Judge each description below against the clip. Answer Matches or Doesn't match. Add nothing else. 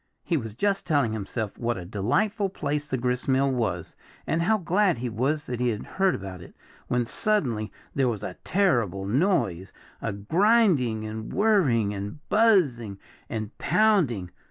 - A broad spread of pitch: Matches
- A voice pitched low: Matches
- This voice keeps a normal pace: Matches